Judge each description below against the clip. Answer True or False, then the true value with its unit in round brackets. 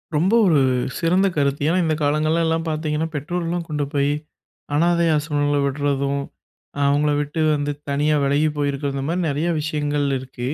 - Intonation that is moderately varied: False (2.2 semitones)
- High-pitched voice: False (150 Hz)